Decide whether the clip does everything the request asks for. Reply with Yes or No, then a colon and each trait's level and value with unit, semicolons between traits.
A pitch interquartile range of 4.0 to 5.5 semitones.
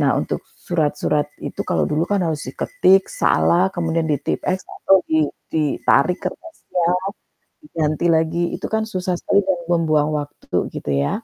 No: average, 3.4 semitones